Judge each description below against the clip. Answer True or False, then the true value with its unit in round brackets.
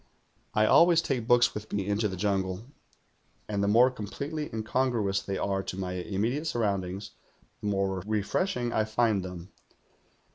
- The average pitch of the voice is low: True (105 Hz)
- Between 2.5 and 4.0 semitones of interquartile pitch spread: True (3.7 semitones)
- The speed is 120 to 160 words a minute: True (150 wpm)